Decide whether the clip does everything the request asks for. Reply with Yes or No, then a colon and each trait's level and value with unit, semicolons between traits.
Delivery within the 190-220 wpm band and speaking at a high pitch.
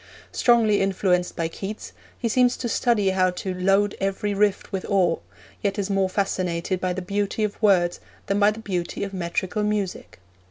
No: average, 175 wpm; high, 195 Hz